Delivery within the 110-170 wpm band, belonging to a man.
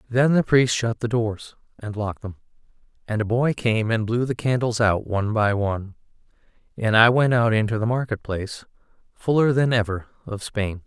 No: average, 190 wpm; male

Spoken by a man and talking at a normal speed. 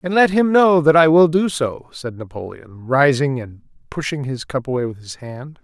No: male; fast, 215 wpm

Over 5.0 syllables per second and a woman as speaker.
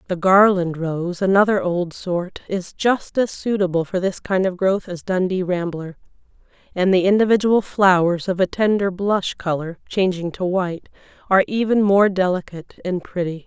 No: 4.9 syllables/s; female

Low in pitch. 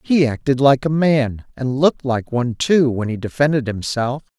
Yes: low, 130 Hz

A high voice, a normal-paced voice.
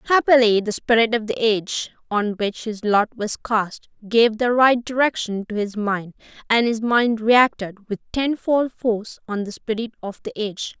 Yes: high, 225 Hz; average, 180 wpm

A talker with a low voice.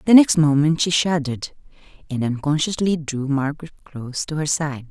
No: medium, 150 Hz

